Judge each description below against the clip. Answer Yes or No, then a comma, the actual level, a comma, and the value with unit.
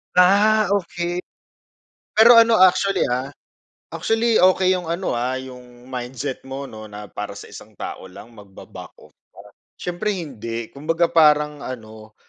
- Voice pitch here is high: No, medium, 145 Hz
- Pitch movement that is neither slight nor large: No, wide, 7.5 semitones